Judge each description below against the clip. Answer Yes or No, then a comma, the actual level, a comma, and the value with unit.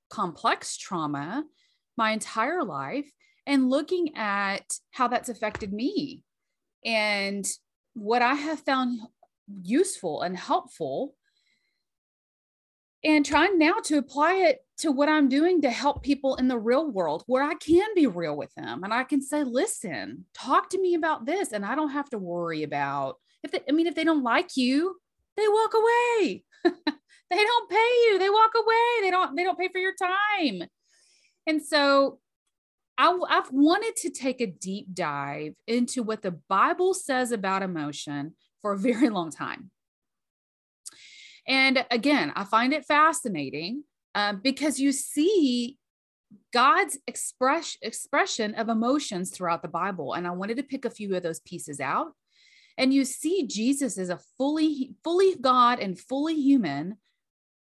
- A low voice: No, very high, 275 Hz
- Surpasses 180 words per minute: No, average, 160 wpm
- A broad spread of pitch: Yes, wide, 7.1 semitones